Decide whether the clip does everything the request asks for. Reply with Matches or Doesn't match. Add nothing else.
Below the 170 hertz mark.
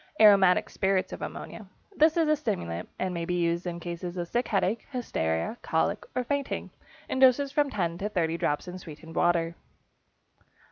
Doesn't match